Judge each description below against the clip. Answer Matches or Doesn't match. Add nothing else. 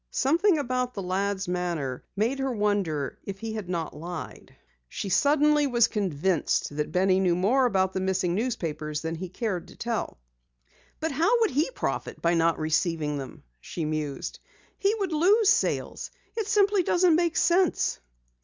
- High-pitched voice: Matches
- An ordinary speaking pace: Matches